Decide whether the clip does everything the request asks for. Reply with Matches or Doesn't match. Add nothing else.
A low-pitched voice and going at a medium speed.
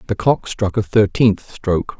Matches